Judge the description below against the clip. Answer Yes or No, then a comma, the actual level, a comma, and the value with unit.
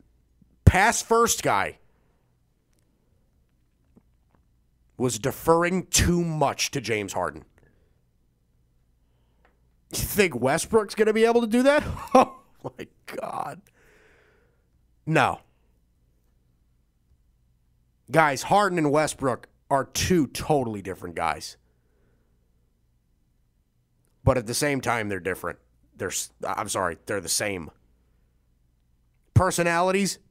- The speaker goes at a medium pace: No, slow, 90 wpm